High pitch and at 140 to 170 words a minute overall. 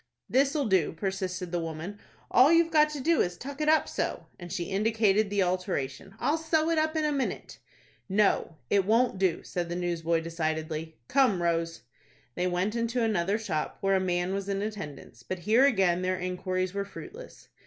No: high, 195 Hz; average, 190 wpm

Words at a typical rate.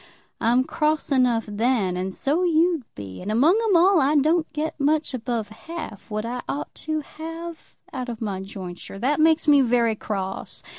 Yes: average, 180 wpm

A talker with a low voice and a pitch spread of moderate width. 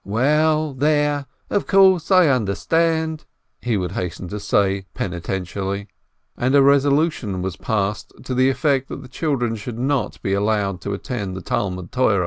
No: low, 125 Hz; wide, 6.8 semitones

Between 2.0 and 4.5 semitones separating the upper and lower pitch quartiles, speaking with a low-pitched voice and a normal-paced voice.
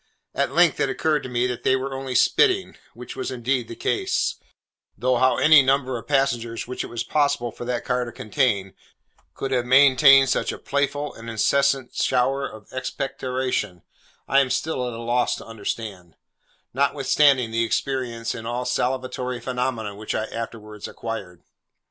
Yes: average, 2.7 semitones; low, 125 Hz; average, 165 wpm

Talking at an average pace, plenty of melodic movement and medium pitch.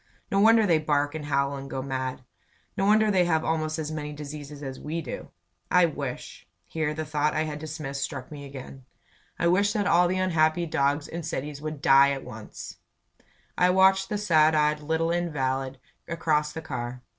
No: average, 190 wpm; average, 3.3 semitones; medium, 155 Hz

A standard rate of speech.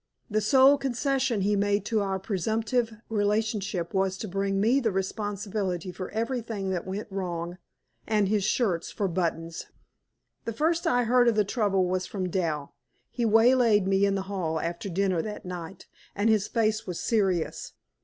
Yes: average, 165 wpm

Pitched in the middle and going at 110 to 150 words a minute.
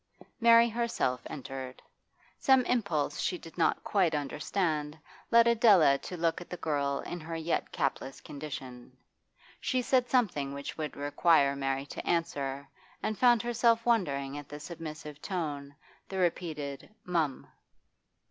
Yes: medium, 160 Hz; average, 140 wpm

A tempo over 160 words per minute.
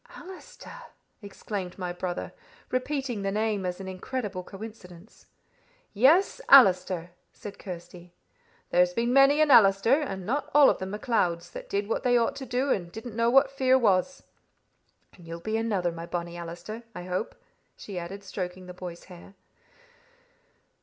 No: average, 155 wpm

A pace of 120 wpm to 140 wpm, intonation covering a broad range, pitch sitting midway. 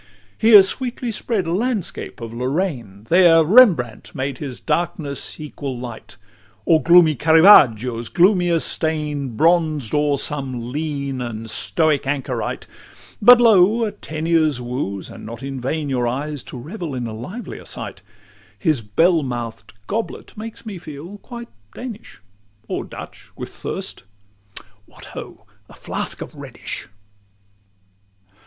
Yes: slow, 135 wpm; wide, 6.2 semitones; medium, 150 Hz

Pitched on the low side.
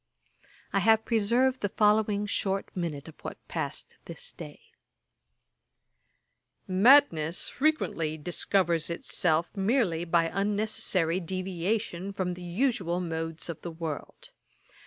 No: medium, 185 Hz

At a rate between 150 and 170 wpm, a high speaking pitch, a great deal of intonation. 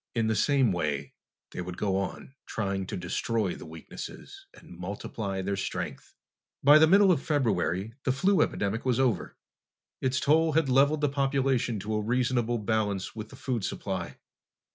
No: average, 165 wpm; low, 115 Hz; wide, 5.7 semitones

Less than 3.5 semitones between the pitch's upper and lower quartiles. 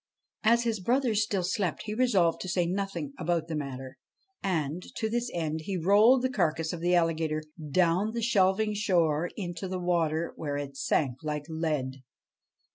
No: average, 4.7 semitones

